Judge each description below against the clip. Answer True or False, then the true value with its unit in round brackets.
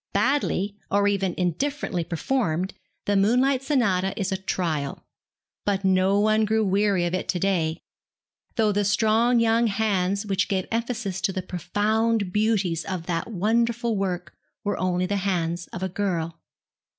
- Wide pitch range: False (3.2 semitones)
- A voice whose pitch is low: False (195 Hz)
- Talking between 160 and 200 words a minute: False (150 wpm)